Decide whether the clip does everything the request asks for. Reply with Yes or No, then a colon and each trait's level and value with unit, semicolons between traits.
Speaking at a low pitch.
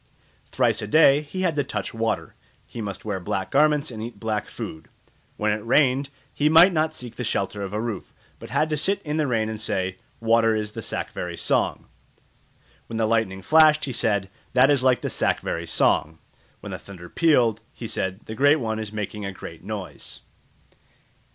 Yes: low, 115 Hz